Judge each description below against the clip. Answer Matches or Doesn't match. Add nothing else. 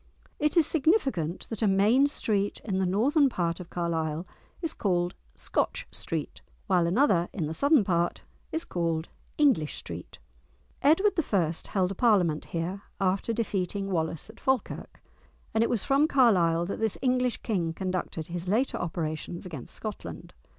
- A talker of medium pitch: Doesn't match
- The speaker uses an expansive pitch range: Matches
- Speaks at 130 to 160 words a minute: Matches